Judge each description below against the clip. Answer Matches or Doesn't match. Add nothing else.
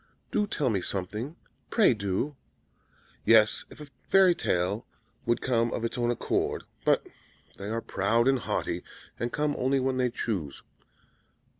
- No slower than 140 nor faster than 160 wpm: Matches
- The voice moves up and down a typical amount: Matches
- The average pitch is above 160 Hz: Doesn't match